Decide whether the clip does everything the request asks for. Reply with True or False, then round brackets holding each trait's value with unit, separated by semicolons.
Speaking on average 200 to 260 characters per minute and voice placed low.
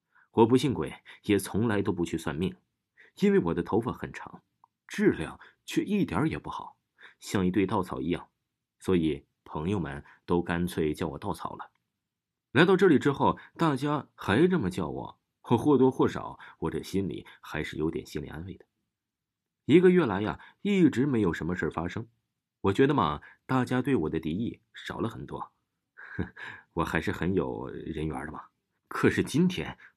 True (240 characters per minute; 115 Hz)